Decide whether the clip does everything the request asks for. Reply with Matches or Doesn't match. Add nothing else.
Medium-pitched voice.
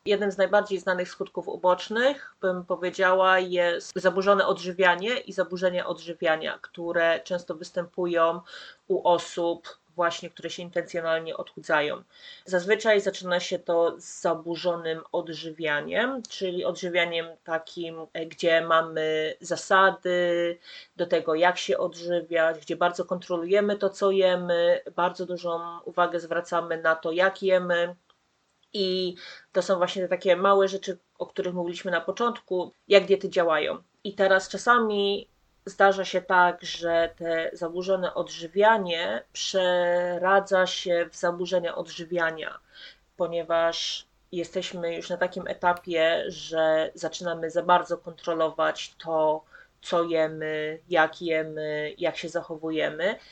Matches